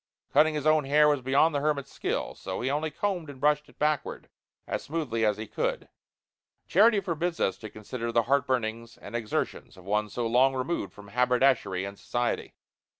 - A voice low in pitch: Yes, low, 130 Hz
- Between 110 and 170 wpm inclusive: No, average, 185 wpm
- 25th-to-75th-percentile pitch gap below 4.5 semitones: No, average, 4.8 semitones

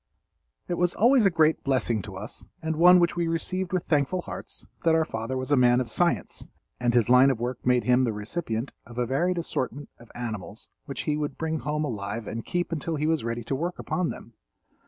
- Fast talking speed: Yes, fast, 220 wpm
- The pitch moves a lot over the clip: Yes, wide, 5.8 semitones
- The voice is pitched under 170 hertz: Yes, medium, 140 Hz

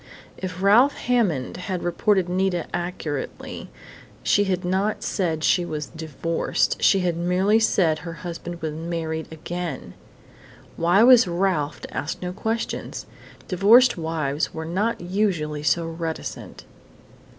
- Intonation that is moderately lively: Yes, average, 3.1 semitones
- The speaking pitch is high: No, medium, 175 Hz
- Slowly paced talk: Yes, slow, 130 wpm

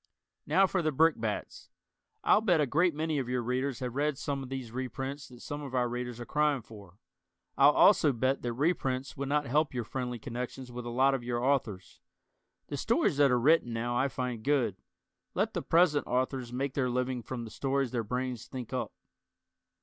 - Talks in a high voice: No, low, 130 Hz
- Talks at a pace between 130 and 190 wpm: No, average, 200 wpm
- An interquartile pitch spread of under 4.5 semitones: Yes, average, 2.8 semitones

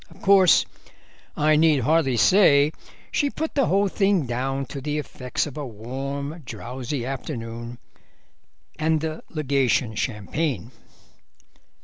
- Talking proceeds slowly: Yes, slow, 120 wpm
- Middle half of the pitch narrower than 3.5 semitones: No, average, 4.2 semitones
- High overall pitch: No, medium, 140 Hz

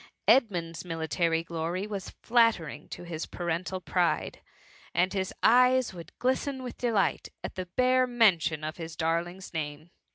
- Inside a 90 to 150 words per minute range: Yes, average, 140 wpm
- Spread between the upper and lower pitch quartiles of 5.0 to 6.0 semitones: Yes, wide, 5.6 semitones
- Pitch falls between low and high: Yes, medium, 180 Hz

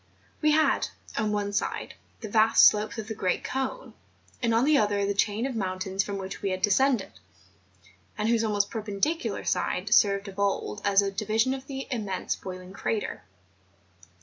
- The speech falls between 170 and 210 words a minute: Yes, average, 175 wpm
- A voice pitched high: Yes, high, 210 Hz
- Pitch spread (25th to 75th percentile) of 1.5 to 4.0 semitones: Yes, average, 2.7 semitones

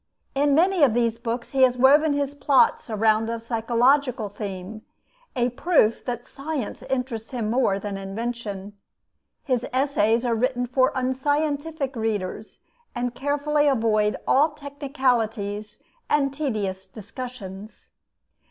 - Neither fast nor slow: No, slow, 125 wpm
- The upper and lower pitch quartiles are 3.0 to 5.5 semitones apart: Yes, average, 4.0 semitones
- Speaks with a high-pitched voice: Yes, high, 245 Hz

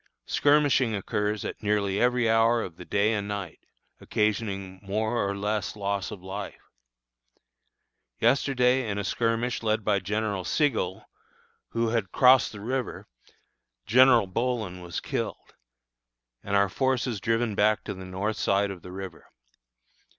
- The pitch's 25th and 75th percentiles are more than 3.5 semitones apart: No, average, 3.0 semitones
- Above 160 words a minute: No, average, 140 wpm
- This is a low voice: Yes, low, 105 Hz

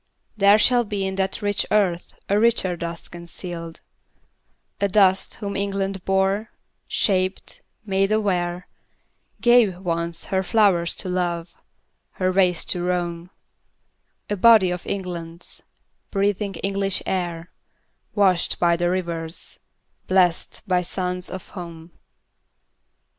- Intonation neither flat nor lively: No, narrow, 2.3 semitones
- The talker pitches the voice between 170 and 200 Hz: Yes, medium, 185 Hz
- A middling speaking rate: No, slow, 115 wpm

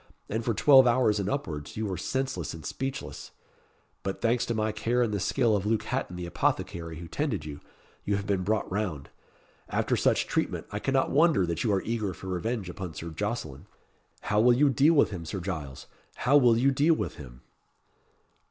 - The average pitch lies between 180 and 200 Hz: No, low, 105 Hz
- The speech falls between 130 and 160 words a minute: No, average, 200 wpm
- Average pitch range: No, wide, 5.7 semitones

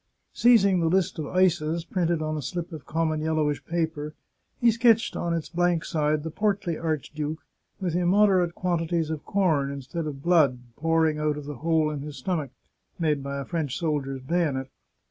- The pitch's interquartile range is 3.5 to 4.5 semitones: No, average, 2.7 semitones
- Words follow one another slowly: No, average, 175 wpm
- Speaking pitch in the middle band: Yes, medium, 160 Hz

